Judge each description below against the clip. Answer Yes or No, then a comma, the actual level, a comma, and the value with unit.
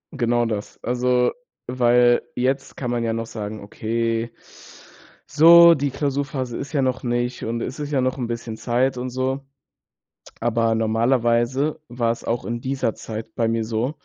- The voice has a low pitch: Yes, low, 120 Hz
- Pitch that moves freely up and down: No, narrow, 2.4 semitones